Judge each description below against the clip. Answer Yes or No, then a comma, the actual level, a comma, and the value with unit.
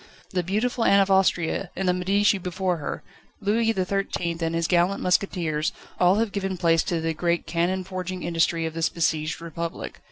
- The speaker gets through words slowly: No, average, 180 wpm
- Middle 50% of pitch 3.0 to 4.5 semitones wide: No, narrow, 2.5 semitones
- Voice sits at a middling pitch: Yes, medium, 180 Hz